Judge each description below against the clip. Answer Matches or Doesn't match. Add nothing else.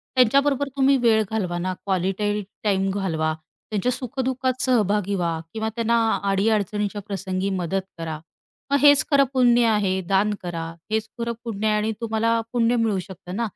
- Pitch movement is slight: Doesn't match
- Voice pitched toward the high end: Matches